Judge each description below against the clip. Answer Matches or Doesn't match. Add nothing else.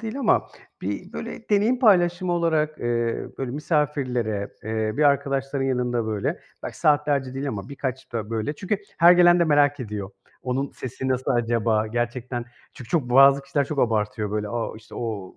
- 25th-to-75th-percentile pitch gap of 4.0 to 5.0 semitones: Matches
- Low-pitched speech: Matches